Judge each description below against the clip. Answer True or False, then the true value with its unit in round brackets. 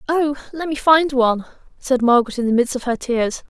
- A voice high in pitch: True (260 Hz)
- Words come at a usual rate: False (220 wpm)